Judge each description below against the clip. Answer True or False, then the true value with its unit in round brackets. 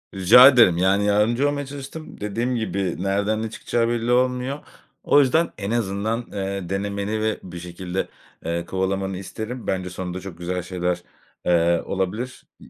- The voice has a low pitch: True (100 Hz)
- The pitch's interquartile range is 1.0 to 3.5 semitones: False (4.3 semitones)